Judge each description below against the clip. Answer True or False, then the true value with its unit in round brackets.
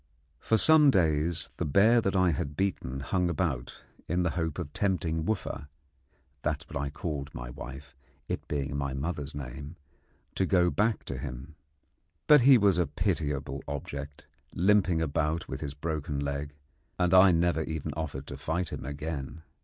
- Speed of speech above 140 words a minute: True (170 wpm)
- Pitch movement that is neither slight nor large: True (4.1 semitones)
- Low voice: True (80 Hz)